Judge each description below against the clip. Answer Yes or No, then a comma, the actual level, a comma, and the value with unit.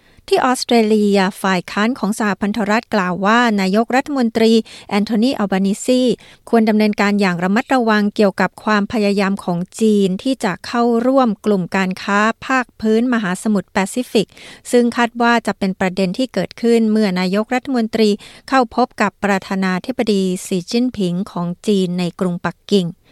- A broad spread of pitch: No, average, 3.5 semitones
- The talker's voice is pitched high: Yes, high, 210 Hz